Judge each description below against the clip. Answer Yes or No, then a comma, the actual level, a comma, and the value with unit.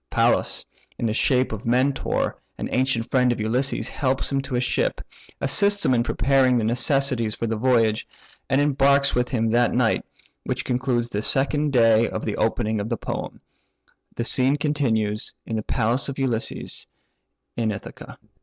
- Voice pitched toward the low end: Yes, low, 125 Hz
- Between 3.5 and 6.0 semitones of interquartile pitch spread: No, average, 3.0 semitones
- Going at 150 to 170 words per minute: Yes, average, 165 wpm